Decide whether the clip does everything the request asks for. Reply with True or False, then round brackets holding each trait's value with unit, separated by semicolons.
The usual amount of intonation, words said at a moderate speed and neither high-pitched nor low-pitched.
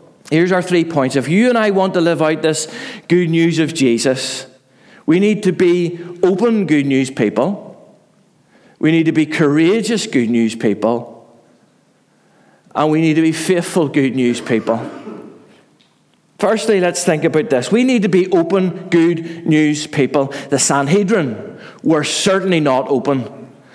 True (5.0 semitones; 155 wpm; 160 Hz)